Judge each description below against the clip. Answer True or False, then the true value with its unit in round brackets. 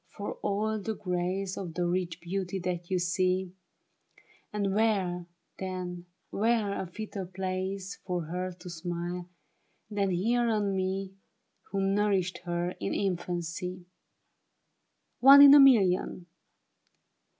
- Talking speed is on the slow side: True (120 wpm)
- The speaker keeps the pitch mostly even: True (2.0 semitones)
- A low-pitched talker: False (185 Hz)